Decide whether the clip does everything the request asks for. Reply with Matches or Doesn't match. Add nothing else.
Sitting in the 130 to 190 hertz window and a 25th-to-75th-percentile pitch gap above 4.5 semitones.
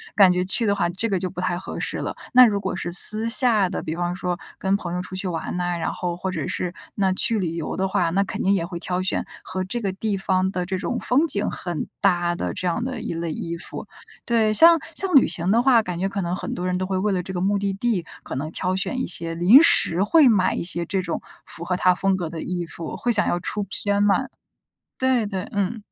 Doesn't match